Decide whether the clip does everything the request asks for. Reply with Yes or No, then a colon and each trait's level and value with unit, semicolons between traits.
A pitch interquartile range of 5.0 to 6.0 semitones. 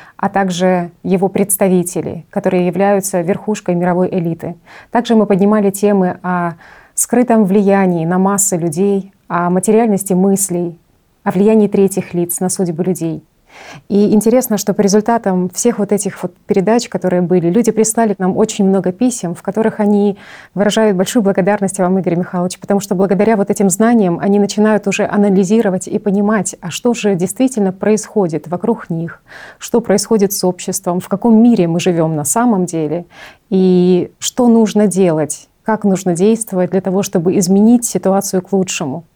No: narrow, 2.5 semitones